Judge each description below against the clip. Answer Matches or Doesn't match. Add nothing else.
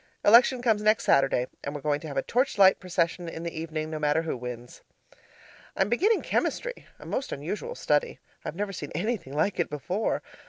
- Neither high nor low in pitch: Matches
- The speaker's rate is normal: Matches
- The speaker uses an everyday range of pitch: Doesn't match